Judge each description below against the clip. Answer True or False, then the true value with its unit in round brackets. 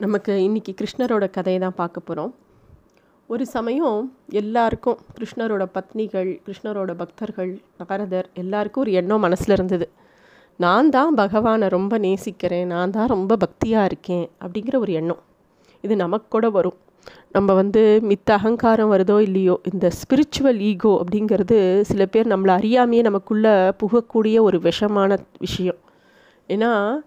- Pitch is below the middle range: False (205 Hz)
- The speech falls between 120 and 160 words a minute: True (125 wpm)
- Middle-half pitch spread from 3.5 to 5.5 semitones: False (3.1 semitones)